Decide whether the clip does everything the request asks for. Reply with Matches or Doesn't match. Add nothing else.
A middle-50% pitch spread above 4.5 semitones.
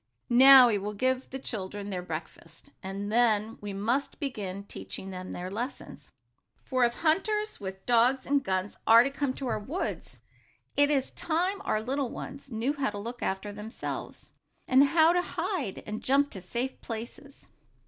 Matches